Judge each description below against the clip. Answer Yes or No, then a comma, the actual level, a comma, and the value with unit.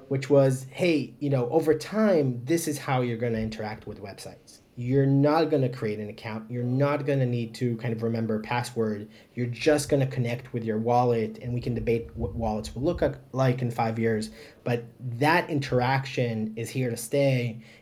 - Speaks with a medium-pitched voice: No, low, 120 Hz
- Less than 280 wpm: Yes, average, 200 wpm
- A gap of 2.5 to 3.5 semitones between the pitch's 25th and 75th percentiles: Yes, average, 3.2 semitones